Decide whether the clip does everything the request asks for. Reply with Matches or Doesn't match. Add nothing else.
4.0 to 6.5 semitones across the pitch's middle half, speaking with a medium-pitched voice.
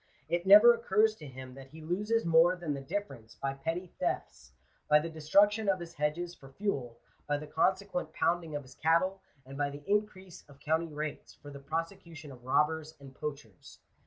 Matches